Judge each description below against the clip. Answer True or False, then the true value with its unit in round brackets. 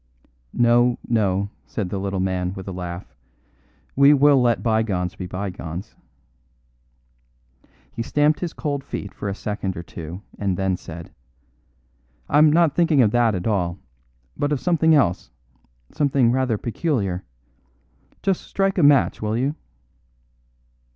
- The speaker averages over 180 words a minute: False (135 wpm)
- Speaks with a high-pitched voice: False (110 Hz)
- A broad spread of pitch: True (7.2 semitones)